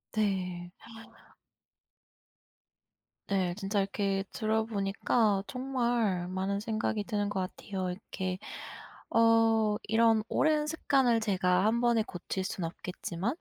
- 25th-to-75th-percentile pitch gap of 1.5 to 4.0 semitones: Yes, average, 3.2 semitones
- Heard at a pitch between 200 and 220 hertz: Yes, high, 205 Hz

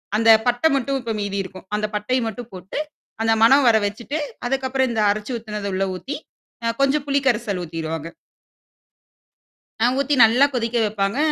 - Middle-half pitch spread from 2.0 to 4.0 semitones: No, average, 4.4 semitones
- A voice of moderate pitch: No, high, 225 Hz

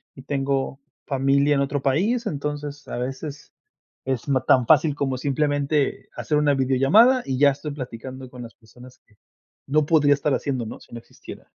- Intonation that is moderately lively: No, narrow, 2.1 semitones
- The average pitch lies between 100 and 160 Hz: Yes, medium, 140 Hz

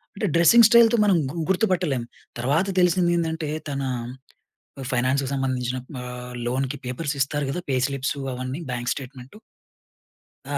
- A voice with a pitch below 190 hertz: Yes, medium, 140 Hz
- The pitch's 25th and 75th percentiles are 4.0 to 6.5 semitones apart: Yes, average, 5.2 semitones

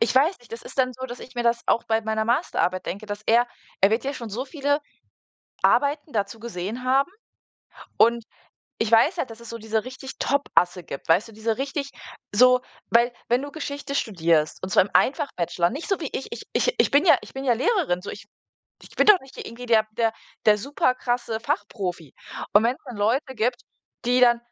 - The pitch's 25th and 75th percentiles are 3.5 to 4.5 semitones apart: Yes, average, 3.8 semitones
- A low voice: No, high, 235 Hz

